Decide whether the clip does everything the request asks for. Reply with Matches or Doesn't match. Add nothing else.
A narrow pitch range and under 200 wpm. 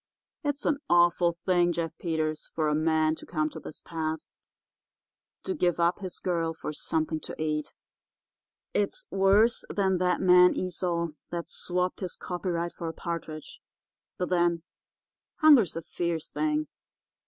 Matches